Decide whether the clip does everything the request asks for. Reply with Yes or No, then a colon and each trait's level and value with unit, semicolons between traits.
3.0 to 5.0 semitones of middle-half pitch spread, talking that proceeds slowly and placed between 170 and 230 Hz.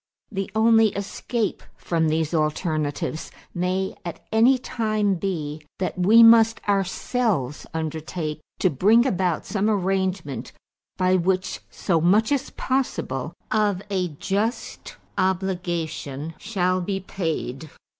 Yes: average, 4.5 semitones; slow, 115 wpm; medium, 185 Hz